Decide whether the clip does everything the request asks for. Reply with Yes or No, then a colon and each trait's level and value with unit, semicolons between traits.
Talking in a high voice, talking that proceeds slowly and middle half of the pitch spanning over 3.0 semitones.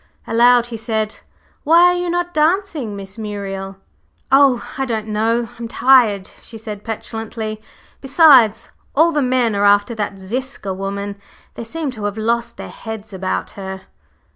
No: high, 225 Hz; average, 155 wpm; average, 4.4 semitones